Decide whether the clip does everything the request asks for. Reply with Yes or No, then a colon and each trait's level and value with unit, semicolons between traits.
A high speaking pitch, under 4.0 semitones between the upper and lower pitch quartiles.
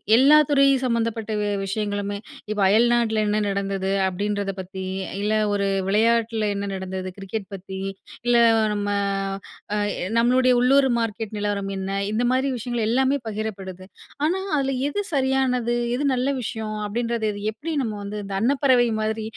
Yes: high, 220 Hz; average, 3.4 semitones